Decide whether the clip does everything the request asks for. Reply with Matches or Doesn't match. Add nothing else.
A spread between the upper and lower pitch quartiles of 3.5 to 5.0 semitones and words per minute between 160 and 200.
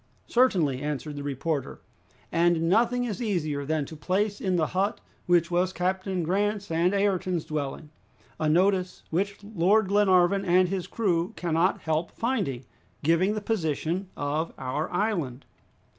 Doesn't match